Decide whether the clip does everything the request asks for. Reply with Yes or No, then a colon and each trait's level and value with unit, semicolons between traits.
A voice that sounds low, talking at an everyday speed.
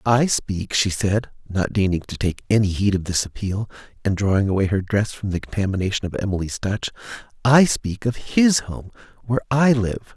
Yes: low, 105 Hz; average, 185 wpm